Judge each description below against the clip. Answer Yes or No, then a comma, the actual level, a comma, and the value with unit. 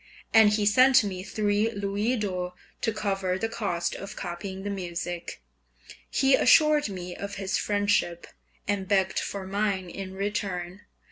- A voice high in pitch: Yes, high, 200 Hz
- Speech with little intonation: Yes, narrow, 2.0 semitones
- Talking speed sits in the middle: Yes, average, 145 wpm